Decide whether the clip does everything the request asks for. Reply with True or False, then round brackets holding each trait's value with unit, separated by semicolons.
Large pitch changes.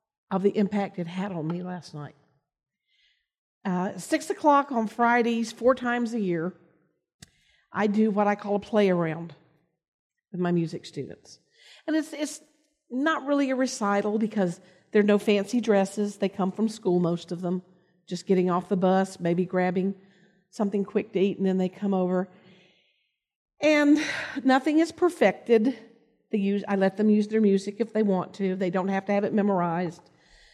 False (4.1 semitones)